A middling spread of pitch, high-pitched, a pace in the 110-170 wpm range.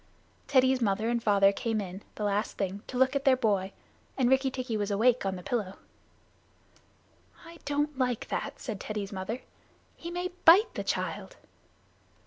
Yes: average, 4.8 semitones; high, 230 Hz; average, 165 wpm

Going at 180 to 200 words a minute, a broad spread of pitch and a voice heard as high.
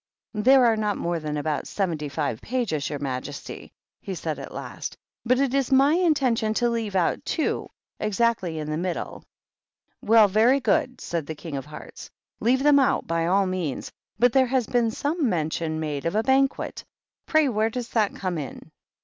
Yes: average, 185 wpm; wide, 7.9 semitones; high, 215 Hz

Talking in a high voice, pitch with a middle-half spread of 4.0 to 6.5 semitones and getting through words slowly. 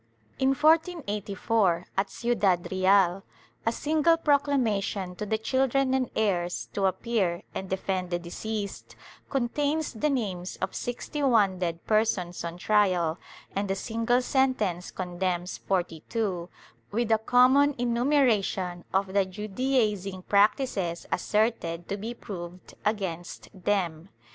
Yes: high, 205 Hz; average, 4.9 semitones; slow, 125 wpm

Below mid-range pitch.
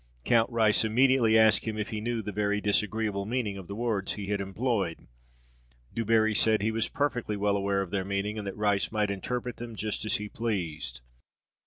Yes: low, 105 Hz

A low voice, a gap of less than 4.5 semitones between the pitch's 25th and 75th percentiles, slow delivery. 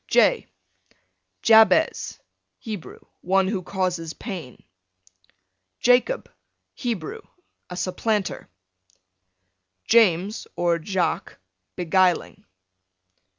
No: high, 190 Hz; average, 3.9 semitones; slow, 65 wpm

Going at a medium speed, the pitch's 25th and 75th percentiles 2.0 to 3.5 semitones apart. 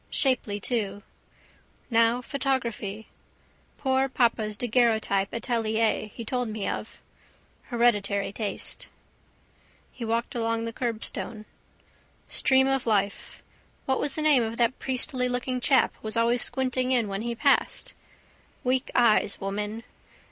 No: slow, 120 wpm; average, 2.8 semitones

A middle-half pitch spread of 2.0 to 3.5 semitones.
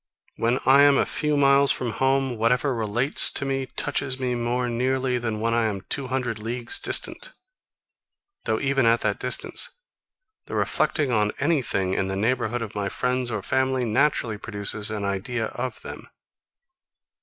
Yes: average, 3.1 semitones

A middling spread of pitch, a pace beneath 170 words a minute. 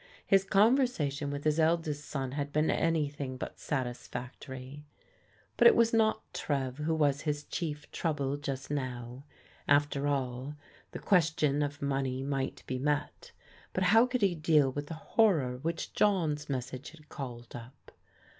Yes: average, 3.2 semitones; average, 155 wpm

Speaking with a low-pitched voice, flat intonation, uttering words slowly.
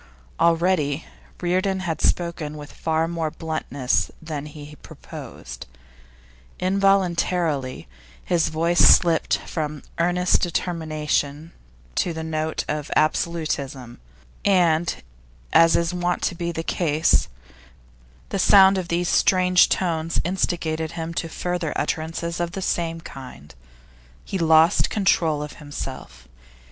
No: medium, 165 Hz; narrow, 2.3 semitones; slow, 115 wpm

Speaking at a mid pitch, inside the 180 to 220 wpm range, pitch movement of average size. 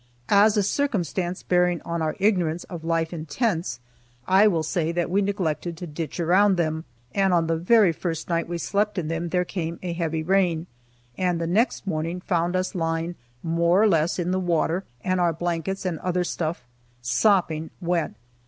No: medium, 175 Hz; average, 185 wpm; narrow, 2.3 semitones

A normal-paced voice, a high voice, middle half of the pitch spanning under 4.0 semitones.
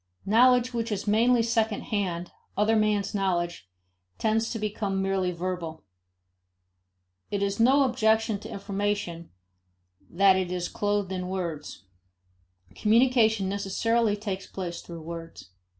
No: slow, 120 wpm; high, 200 Hz; average, 3.3 semitones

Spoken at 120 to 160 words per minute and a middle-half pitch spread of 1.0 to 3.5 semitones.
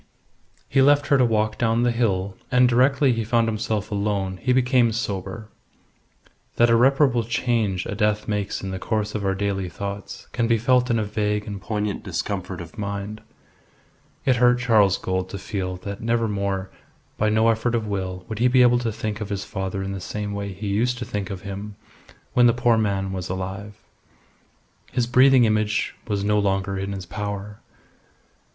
No: average, 185 wpm; average, 3.1 semitones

